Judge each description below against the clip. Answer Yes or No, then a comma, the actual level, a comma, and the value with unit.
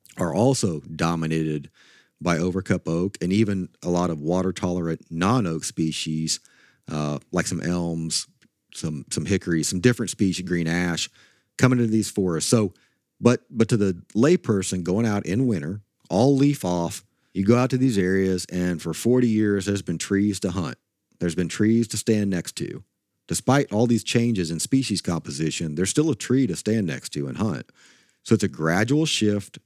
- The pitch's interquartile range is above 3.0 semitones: Yes, average, 4.7 semitones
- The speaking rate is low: No, average, 180 wpm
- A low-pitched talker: Yes, very low, 95 Hz